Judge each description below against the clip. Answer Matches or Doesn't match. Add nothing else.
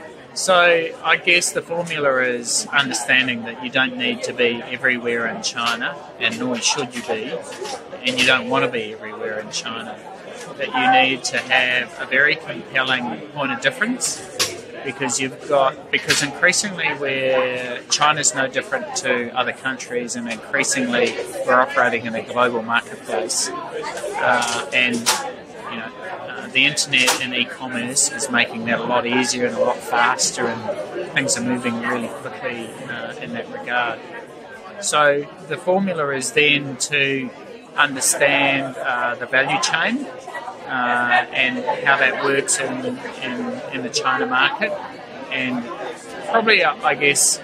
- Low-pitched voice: Matches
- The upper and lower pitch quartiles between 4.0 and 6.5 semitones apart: Doesn't match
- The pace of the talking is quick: Doesn't match